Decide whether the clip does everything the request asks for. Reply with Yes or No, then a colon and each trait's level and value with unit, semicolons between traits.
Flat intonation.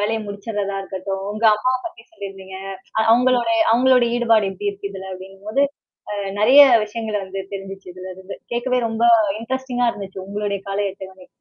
No: average, 3.3 semitones